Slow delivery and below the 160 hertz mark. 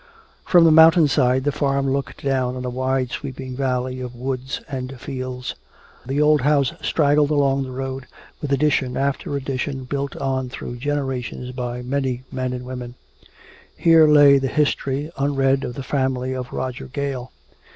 No: average, 160 wpm; low, 135 Hz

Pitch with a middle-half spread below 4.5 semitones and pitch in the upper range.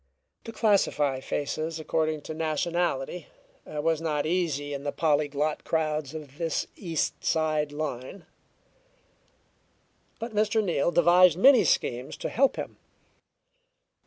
No: average, 3.0 semitones; medium, 155 Hz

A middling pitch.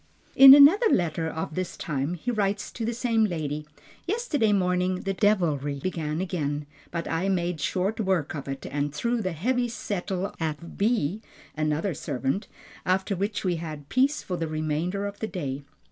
Yes: medium, 180 Hz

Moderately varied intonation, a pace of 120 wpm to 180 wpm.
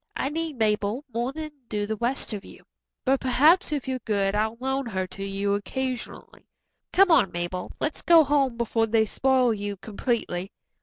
Yes: average, 4.8 semitones; average, 175 wpm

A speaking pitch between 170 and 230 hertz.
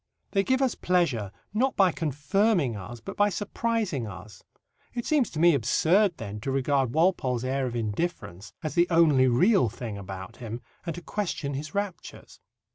No: medium, 145 Hz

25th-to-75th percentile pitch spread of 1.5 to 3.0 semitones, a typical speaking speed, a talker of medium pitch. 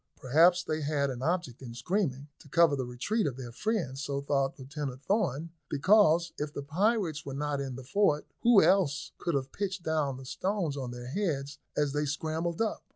No: average, 4.4 semitones; average, 195 wpm; medium, 150 Hz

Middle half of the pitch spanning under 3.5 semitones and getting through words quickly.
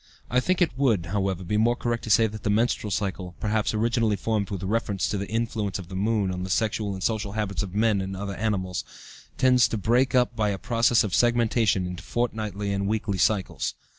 Yes: average, 2.8 semitones; fast, 215 wpm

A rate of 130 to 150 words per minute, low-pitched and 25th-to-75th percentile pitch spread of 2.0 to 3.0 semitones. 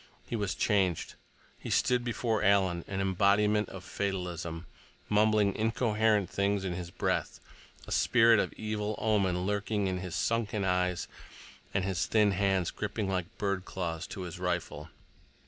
Yes: average, 145 wpm; low, 100 Hz; narrow, 2.5 semitones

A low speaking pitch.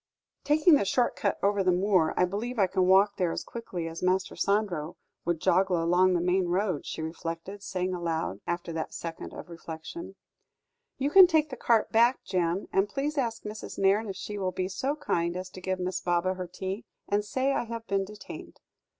No: high, 190 Hz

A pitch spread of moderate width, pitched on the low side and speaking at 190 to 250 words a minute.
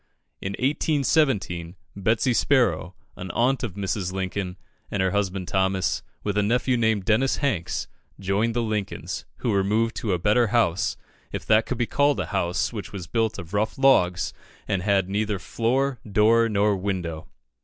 No: average, 3.6 semitones; low, 105 Hz; average, 165 wpm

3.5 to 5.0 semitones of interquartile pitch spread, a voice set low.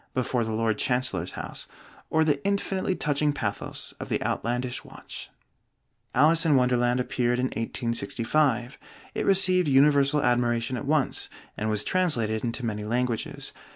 Yes: average, 4.1 semitones; low, 125 Hz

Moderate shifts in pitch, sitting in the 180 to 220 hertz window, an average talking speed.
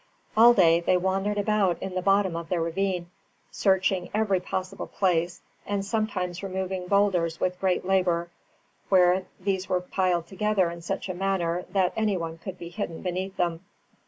No: narrow, 1.8 semitones; medium, 185 Hz; average, 165 wpm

